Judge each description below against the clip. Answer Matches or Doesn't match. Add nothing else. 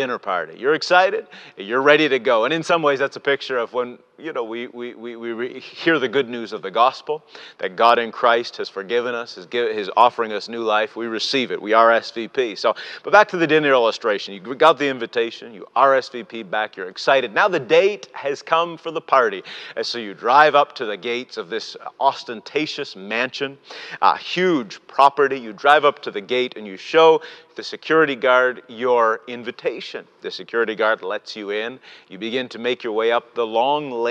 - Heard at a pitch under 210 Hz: Matches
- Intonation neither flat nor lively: Doesn't match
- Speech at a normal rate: Doesn't match